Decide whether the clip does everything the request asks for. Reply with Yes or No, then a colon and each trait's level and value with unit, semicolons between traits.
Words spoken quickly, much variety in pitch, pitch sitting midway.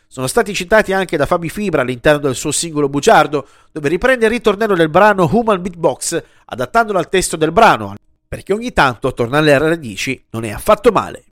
Yes: fast, 185 wpm; wide, 7.2 semitones; medium, 170 Hz